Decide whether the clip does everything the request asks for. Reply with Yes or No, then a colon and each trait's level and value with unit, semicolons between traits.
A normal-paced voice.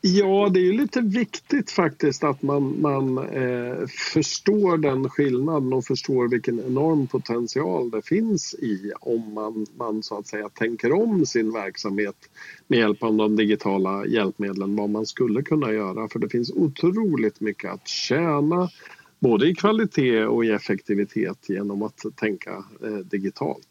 Yes: average, 155 wpm